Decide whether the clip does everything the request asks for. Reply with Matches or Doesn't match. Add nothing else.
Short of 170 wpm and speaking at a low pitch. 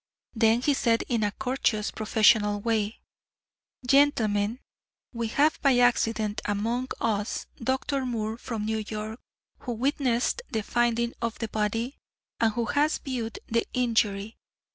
Doesn't match